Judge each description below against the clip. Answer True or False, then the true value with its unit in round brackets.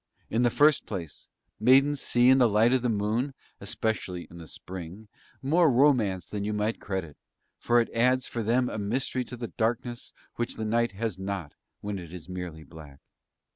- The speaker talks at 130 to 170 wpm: False (185 wpm)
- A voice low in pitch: True (110 Hz)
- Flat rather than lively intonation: False (4.6 semitones)